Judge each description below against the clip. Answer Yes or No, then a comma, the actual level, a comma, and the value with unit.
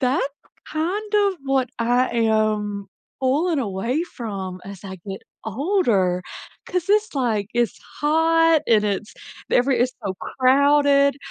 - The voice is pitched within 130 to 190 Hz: No, very high, 255 Hz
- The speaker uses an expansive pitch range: Yes, wide, 6.7 semitones